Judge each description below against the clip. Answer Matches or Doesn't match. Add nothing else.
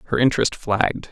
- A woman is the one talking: Doesn't match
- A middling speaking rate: Matches